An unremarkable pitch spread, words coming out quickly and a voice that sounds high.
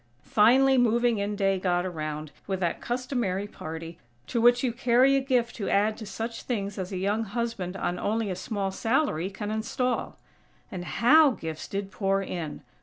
No: average, 4.2 semitones; average, 180 wpm; high, 205 Hz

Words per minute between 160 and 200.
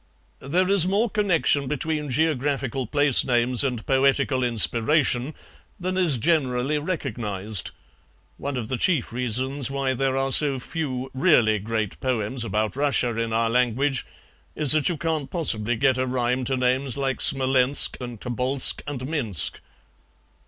No: average, 145 wpm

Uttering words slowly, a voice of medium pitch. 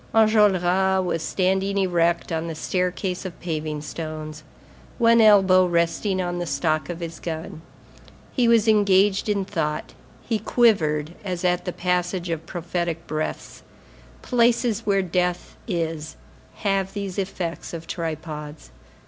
Yes: slow, 130 wpm; medium, 180 Hz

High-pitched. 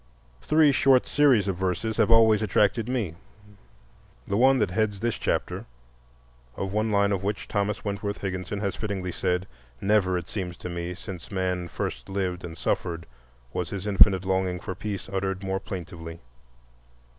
No: very low, 95 Hz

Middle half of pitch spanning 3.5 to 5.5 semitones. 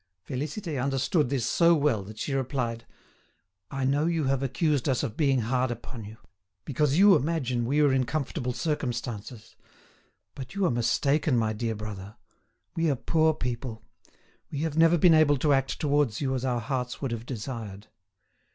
Yes: average, 4.0 semitones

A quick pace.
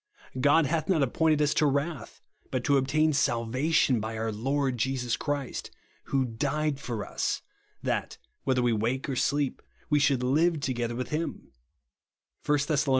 No: average, 155 wpm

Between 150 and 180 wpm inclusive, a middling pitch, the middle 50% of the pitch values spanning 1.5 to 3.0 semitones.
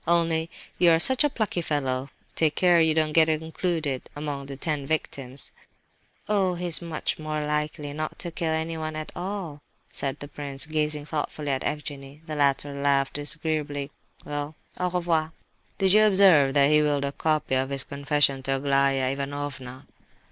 Yes: average, 170 wpm; medium, 150 Hz; narrow, 2.5 semitones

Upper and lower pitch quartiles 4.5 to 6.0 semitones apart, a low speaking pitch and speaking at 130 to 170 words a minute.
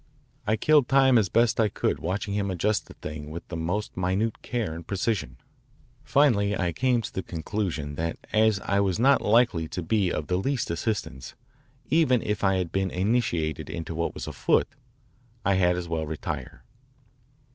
No: average, 5.0 semitones; low, 100 Hz; average, 180 wpm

